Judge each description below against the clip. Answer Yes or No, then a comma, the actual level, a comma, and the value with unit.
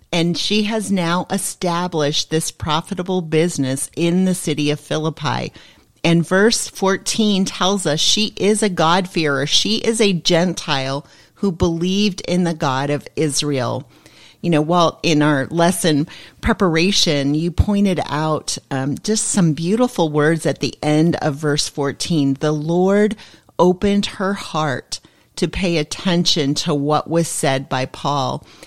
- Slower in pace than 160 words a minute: Yes, average, 145 wpm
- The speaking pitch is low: No, medium, 165 Hz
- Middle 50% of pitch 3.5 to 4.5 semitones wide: Yes, average, 4.0 semitones